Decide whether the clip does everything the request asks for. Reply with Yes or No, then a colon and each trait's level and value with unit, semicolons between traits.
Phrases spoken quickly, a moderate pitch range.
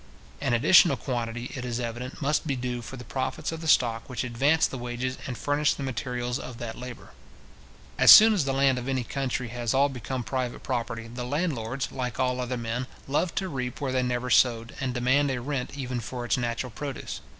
No: fast, 210 wpm; narrow, 2.0 semitones